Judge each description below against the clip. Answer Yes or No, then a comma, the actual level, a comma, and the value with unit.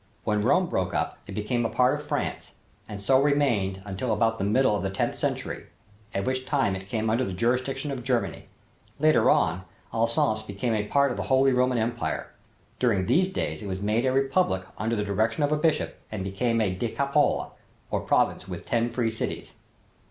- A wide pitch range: No, average, 4.2 semitones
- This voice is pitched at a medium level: No, low, 115 Hz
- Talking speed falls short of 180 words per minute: No, average, 195 wpm